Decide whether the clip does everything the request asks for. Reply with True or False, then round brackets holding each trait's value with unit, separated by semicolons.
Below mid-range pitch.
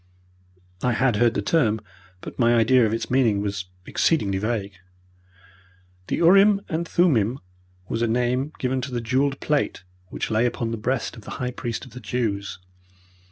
True (120 Hz)